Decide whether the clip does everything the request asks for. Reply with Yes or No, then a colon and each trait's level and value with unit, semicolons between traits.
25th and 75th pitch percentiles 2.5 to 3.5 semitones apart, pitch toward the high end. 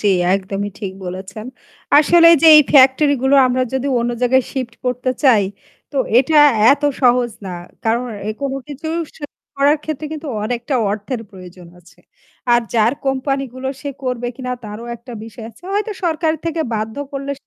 No: average, 4.3 semitones; very high, 255 Hz